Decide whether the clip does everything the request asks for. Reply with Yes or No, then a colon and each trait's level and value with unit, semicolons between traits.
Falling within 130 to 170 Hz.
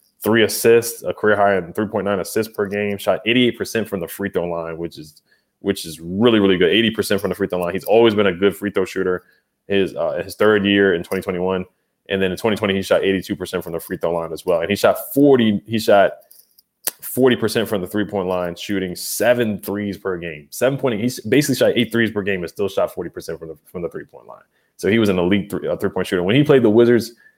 No: low, 100 Hz